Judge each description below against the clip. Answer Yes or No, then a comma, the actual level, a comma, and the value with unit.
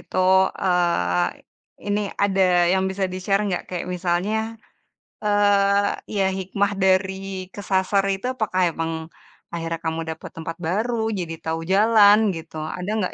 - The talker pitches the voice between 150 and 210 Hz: Yes, high, 190 Hz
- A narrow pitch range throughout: No, average, 3.0 semitones